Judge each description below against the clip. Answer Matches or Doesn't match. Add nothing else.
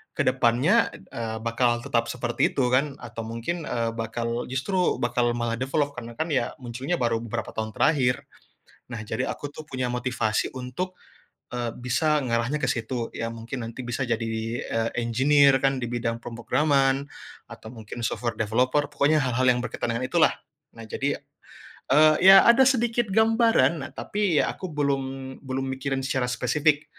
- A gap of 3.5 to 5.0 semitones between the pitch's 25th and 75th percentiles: Matches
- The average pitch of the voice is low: Matches